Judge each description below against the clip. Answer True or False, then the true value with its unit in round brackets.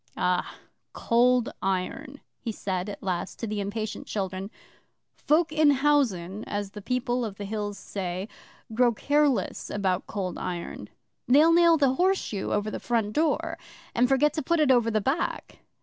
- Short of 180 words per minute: True (160 wpm)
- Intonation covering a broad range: True (5.8 semitones)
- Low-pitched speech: False (225 Hz)